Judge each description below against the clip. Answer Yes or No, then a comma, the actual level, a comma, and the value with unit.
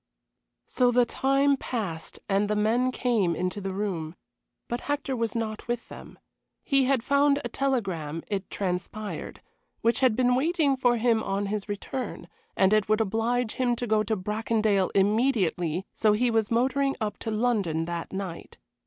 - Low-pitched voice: No, high, 220 Hz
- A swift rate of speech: No, average, 165 wpm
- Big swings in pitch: No, average, 4.0 semitones